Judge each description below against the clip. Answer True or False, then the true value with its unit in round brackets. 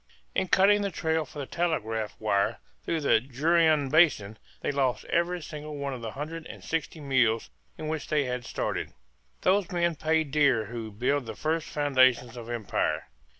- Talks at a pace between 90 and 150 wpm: False (175 wpm)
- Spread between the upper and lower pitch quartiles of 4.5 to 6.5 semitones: True (5.0 semitones)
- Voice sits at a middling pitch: True (145 Hz)